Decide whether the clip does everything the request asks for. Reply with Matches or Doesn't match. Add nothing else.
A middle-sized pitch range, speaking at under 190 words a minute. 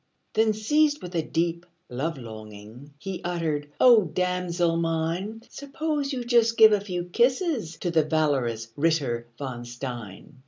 Doesn't match